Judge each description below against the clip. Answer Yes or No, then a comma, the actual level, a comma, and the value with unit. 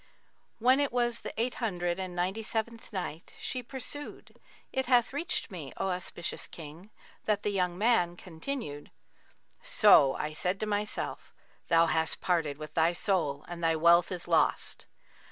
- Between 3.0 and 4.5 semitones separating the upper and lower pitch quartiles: No, wide, 5.5 semitones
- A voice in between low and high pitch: Yes, medium, 180 Hz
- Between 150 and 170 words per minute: Yes, average, 155 wpm